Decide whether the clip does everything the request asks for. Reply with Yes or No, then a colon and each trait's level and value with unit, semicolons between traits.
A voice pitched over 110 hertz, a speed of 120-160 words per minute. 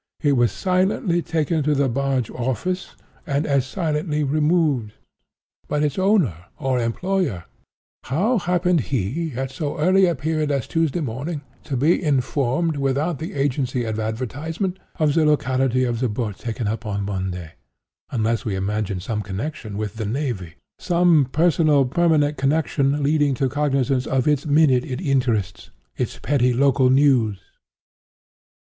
Yes: medium, 140 Hz; average, 140 wpm